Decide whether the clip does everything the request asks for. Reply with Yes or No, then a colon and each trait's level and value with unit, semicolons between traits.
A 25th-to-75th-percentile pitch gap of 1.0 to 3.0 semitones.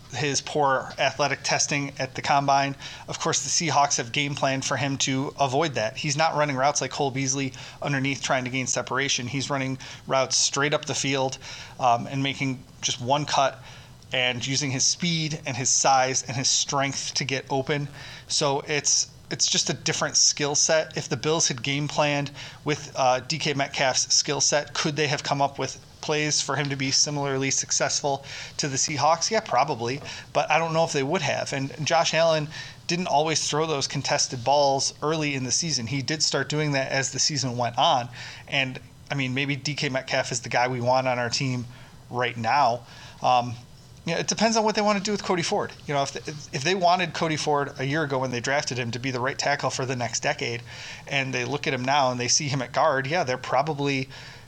Yes: narrow, 2.4 semitones